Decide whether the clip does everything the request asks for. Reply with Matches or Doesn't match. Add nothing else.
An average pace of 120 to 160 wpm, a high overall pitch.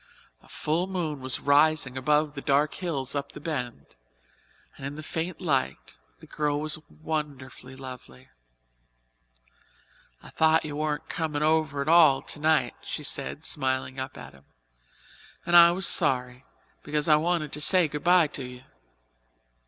Doesn't match